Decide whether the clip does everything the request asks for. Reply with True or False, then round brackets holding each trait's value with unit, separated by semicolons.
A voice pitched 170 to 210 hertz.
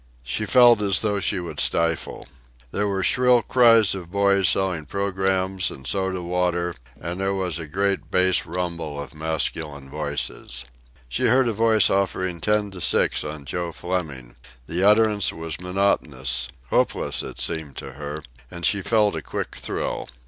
False (90 Hz)